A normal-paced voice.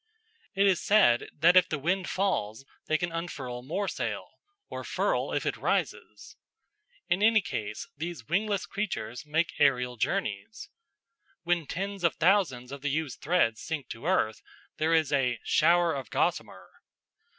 Yes: average, 150 wpm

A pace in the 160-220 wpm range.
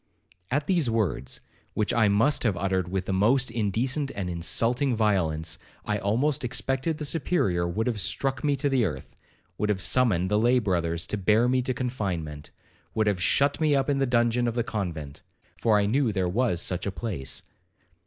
Yes: average, 185 wpm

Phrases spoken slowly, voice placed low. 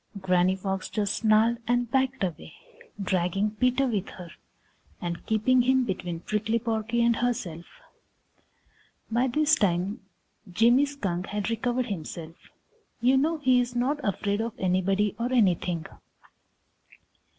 No: slow, 130 wpm; high, 220 Hz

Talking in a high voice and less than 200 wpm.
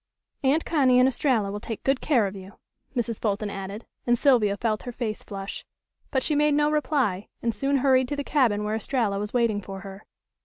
No: high, 235 Hz; fast, 205 wpm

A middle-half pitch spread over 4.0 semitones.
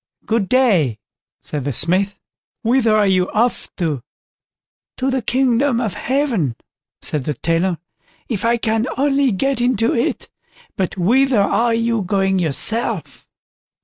Yes: average, 5.2 semitones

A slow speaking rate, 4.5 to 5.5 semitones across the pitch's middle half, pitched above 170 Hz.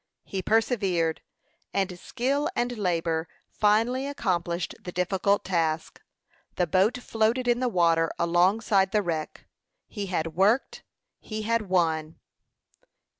Yes: slow, 120 wpm; average, 4.8 semitones; high, 190 Hz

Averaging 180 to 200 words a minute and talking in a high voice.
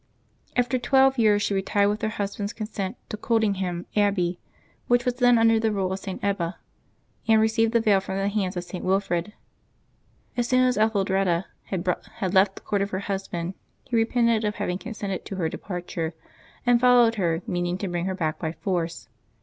Yes: average, 190 wpm; high, 200 Hz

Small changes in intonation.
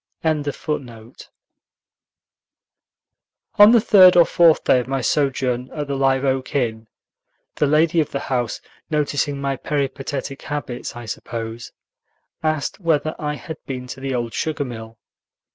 No: average, 3.3 semitones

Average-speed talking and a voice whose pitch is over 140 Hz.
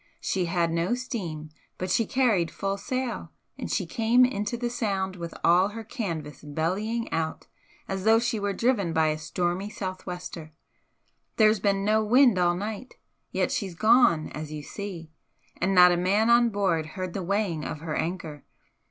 Yes: average, 170 wpm; high, 190 Hz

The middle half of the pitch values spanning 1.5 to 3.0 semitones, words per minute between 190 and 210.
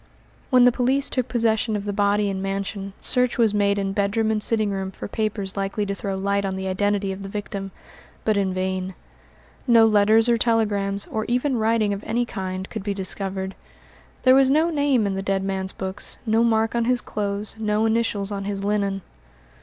Yes: narrow, 2.5 semitones; average, 200 wpm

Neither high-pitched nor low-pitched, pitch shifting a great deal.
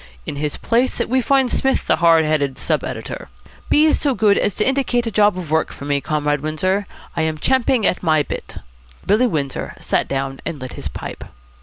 Yes: medium, 175 Hz; wide, 8.2 semitones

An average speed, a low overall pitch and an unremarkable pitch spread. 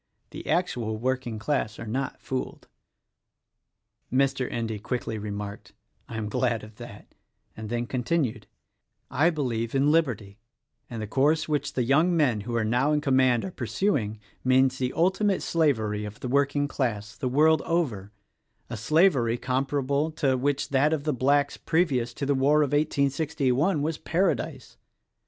Yes: average, 155 wpm; low, 130 Hz; average, 4.2 semitones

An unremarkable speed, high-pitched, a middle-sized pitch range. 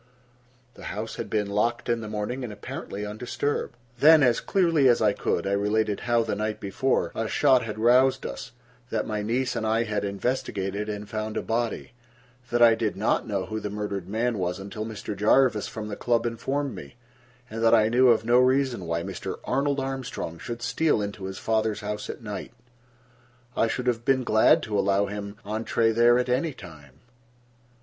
No: average, 190 wpm; low, 110 Hz; average, 3.0 semitones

